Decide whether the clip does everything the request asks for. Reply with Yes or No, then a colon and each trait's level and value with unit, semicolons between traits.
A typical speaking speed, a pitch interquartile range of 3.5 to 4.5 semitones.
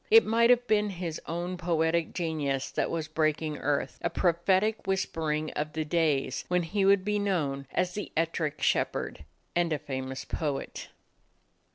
Yes: average, 170 wpm; average, 3.8 semitones